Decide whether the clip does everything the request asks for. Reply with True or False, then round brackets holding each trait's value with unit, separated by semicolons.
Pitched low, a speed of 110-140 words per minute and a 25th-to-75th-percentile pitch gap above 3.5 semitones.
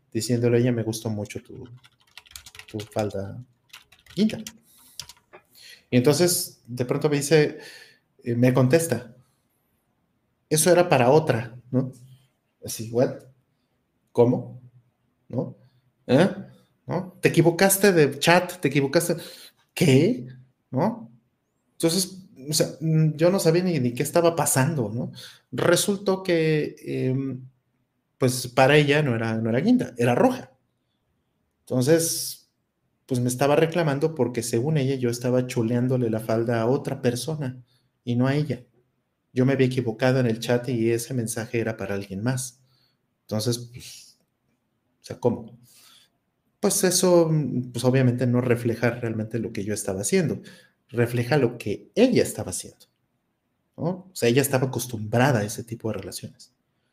True (125 Hz; 135 wpm; 3.9 semitones)